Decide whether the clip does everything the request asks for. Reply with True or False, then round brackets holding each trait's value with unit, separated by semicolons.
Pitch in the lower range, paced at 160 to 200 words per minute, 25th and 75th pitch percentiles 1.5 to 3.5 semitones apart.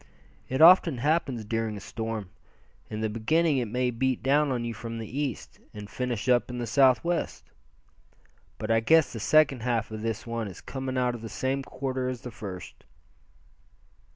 True (120 Hz; 180 wpm; 2.9 semitones)